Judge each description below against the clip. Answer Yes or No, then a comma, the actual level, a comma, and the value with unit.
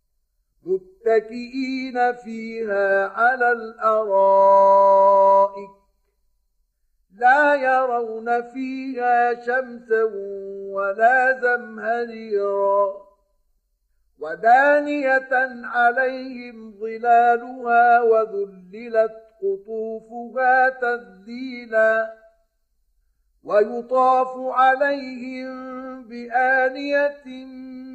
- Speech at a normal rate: No, slow, 40 wpm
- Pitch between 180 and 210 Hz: No, high, 240 Hz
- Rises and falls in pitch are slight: No, average, 3.0 semitones